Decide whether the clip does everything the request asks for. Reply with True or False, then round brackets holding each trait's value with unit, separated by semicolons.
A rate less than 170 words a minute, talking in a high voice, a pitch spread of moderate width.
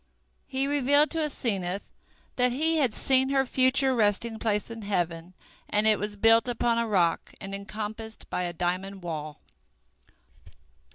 True (150 wpm; 220 Hz; 4.9 semitones)